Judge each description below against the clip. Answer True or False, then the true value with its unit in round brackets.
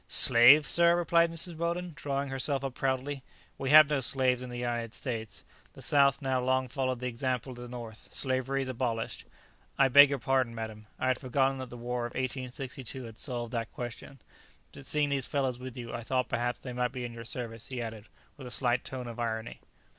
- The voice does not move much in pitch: True (2.3 semitones)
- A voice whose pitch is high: False (130 Hz)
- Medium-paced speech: False (215 wpm)